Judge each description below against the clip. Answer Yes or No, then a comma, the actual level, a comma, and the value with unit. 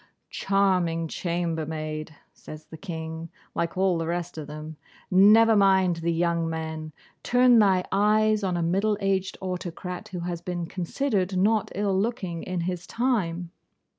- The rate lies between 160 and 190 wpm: No, average, 145 wpm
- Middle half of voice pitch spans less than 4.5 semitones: Yes, average, 2.9 semitones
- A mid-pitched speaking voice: Yes, medium, 180 Hz